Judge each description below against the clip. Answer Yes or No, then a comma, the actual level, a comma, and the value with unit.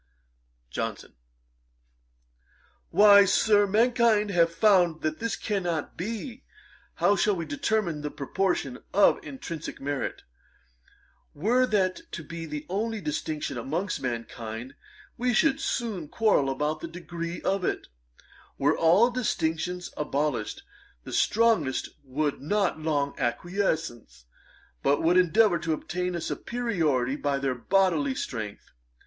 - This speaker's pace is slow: Yes, slow, 120 wpm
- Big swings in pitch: Yes, wide, 6.0 semitones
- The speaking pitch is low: No, medium, 170 Hz